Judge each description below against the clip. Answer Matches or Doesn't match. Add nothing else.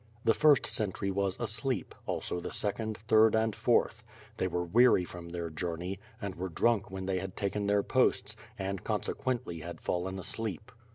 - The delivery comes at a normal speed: Matches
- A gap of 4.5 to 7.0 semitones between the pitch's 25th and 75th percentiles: Doesn't match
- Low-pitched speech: Matches